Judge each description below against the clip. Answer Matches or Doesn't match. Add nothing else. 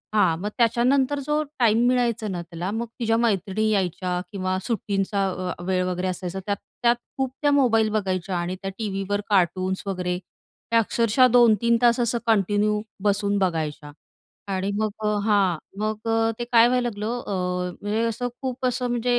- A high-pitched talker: Matches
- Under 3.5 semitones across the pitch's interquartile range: Doesn't match